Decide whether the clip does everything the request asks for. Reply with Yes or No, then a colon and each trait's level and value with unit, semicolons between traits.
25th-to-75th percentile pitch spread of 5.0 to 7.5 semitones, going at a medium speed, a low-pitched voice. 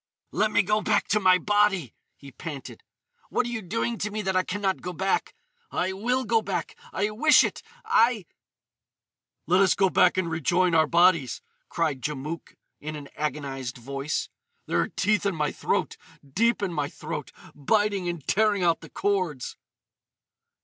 No: average, 5.3 semitones; average, 170 wpm; medium, 185 Hz